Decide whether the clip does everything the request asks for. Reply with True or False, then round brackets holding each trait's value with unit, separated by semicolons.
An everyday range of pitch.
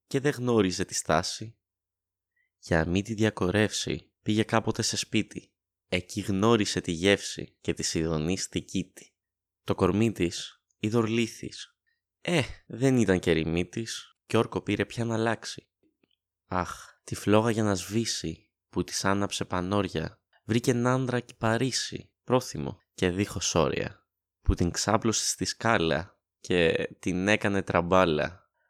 True (3.6 semitones)